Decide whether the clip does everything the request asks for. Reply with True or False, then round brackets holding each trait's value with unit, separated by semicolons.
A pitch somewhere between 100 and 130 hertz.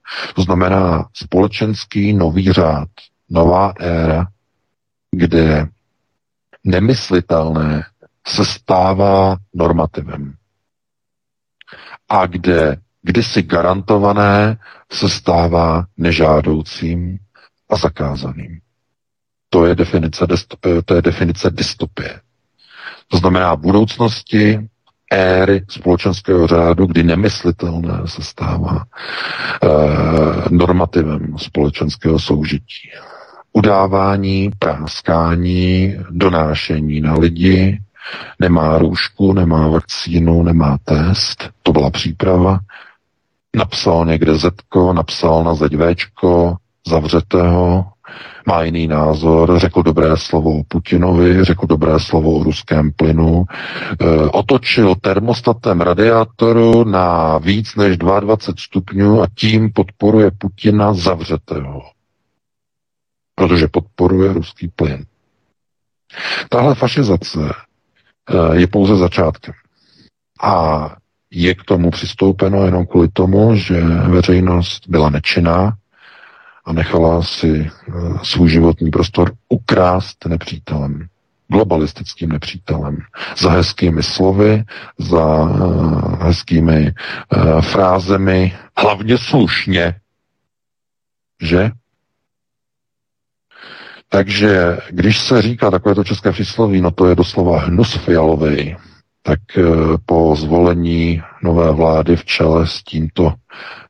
False (90 Hz)